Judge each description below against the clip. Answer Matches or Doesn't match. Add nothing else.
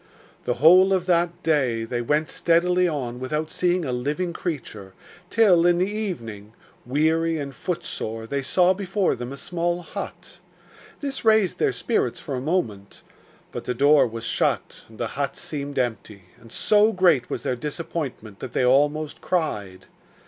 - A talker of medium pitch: Matches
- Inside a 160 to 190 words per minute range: Matches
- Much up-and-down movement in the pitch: Matches